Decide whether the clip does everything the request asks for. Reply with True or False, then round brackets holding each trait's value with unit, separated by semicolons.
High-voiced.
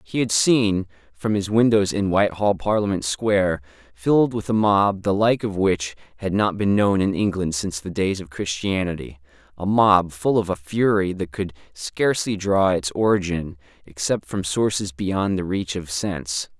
False (95 Hz)